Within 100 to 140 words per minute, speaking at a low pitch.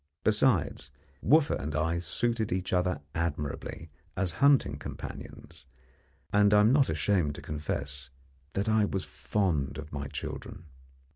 Yes: slow, 135 wpm; very low, 90 Hz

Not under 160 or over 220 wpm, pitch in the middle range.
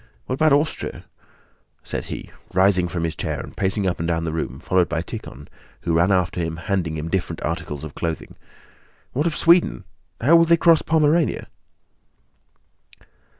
No: average, 165 wpm; very low, 90 Hz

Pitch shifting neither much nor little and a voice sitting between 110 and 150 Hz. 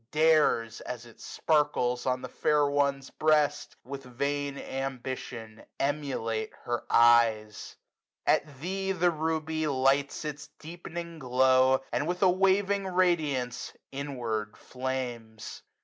Yes: average, 4.1 semitones; medium, 140 Hz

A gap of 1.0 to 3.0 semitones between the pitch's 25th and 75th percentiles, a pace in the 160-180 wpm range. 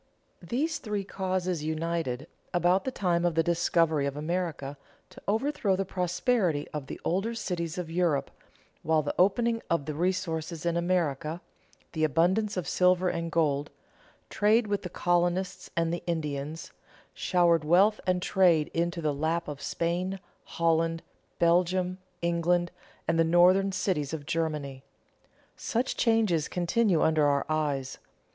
No: average, 2.7 semitones; average, 140 wpm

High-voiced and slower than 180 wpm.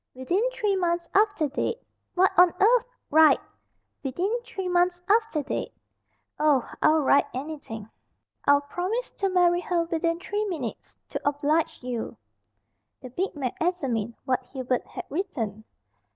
Yes: very high, 330 Hz; average, 140 wpm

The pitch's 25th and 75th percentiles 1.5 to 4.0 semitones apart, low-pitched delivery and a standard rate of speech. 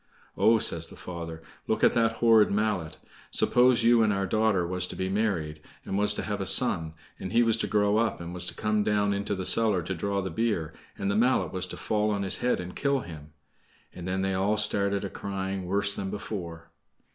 No: average, 2.9 semitones; low, 100 Hz; fast, 225 wpm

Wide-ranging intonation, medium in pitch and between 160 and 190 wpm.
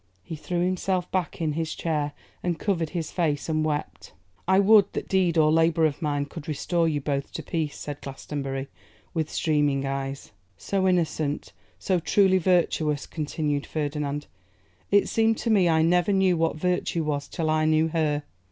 No: average, 3.2 semitones; medium, 160 Hz; average, 170 wpm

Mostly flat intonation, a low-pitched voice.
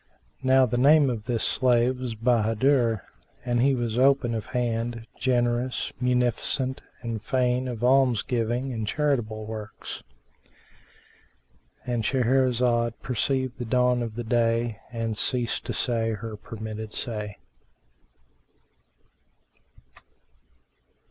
Yes: narrow, 2.1 semitones; low, 120 Hz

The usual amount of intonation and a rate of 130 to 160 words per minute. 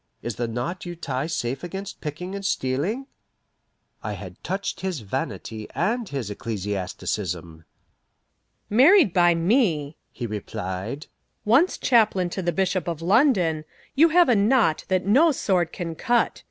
No: wide, 8.2 semitones; average, 140 wpm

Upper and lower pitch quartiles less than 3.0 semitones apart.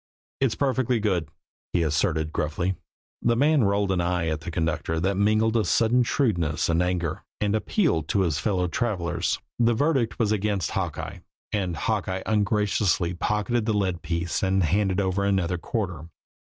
No: average, 4.1 semitones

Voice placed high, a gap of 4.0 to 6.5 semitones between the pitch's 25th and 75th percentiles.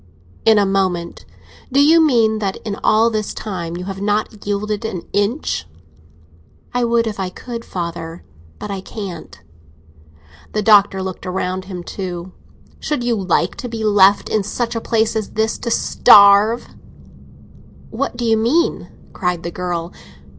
No: high, 205 Hz; average, 3.3 semitones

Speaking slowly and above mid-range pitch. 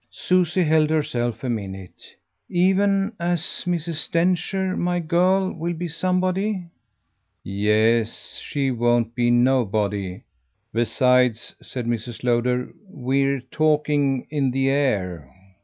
No: slow, 105 wpm; low, 135 Hz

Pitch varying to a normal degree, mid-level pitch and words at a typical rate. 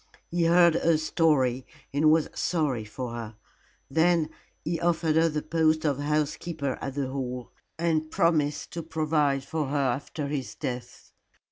Yes: average, 3.0 semitones; medium, 150 Hz; average, 150 wpm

